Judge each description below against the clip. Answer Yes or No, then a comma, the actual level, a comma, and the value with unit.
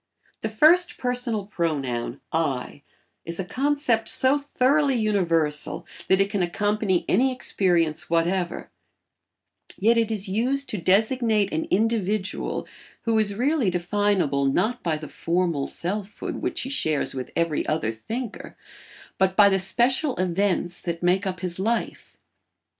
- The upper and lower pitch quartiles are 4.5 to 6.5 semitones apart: Yes, average, 5.2 semitones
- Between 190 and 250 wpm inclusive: No, slow, 135 wpm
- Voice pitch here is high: Yes, high, 195 Hz